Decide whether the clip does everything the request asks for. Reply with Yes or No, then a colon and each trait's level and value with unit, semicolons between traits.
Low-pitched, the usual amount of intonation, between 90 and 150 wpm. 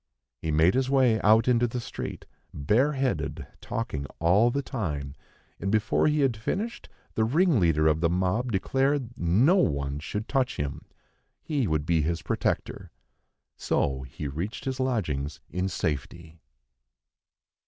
No: low, 105 Hz; wide, 8.5 semitones; average, 145 wpm